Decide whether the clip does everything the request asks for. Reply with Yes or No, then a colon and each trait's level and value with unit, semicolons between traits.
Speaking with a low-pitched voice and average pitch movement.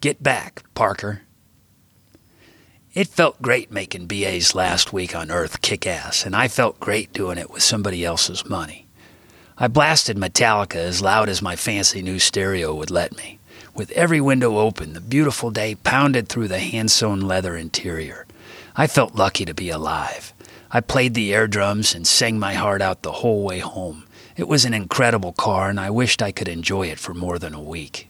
Yes: low, 100 Hz; average, 4.0 semitones